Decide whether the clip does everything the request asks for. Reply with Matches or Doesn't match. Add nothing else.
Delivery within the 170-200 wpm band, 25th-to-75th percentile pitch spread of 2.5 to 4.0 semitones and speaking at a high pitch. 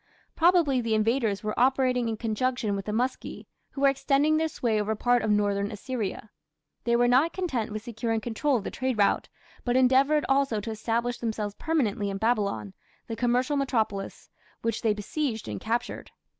Matches